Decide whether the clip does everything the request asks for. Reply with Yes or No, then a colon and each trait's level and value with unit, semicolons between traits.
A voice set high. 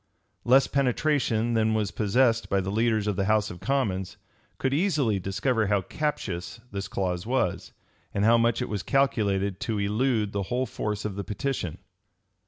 No: low, 110 Hz